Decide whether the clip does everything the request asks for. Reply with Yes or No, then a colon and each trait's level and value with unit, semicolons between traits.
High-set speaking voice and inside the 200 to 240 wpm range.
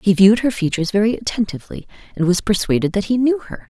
Yes: high, 205 Hz; fast, 205 wpm